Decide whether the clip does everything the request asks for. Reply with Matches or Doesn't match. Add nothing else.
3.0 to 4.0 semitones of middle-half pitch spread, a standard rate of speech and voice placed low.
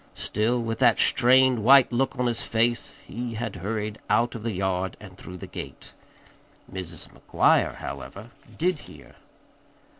Matches